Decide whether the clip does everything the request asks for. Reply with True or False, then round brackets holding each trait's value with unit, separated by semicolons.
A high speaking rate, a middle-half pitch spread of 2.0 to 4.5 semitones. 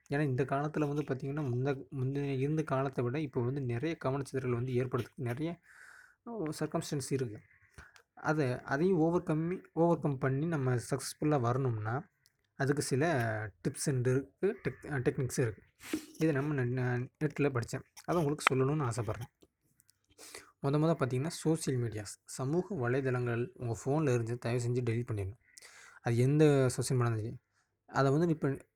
True (135 wpm; 3.6 semitones)